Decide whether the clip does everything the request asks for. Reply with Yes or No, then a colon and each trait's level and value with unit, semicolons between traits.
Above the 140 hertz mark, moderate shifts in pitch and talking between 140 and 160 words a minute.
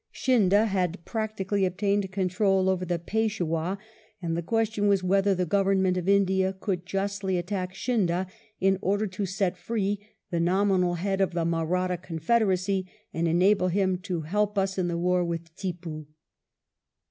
No: high, 190 Hz; narrow, 2.1 semitones; average, 155 wpm